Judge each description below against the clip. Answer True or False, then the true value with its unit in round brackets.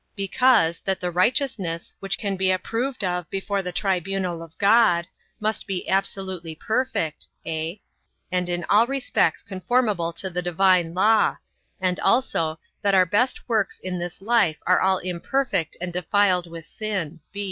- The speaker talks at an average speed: True (150 wpm)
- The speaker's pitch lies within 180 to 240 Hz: True (185 Hz)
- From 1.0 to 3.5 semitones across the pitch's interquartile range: True (3.1 semitones)